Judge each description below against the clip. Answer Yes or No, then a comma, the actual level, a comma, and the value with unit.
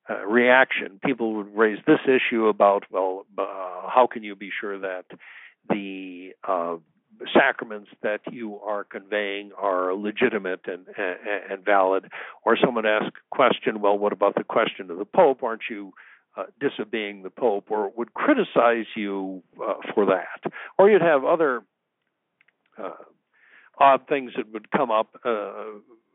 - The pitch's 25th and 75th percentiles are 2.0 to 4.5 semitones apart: Yes, average, 3.2 semitones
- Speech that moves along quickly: No, average, 160 wpm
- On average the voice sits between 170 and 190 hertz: No, low, 105 Hz